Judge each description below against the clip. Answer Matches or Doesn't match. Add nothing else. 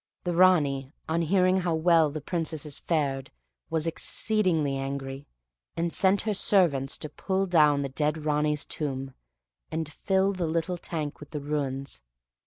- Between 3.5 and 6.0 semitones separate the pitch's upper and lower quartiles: Matches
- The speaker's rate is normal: Matches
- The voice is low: Doesn't match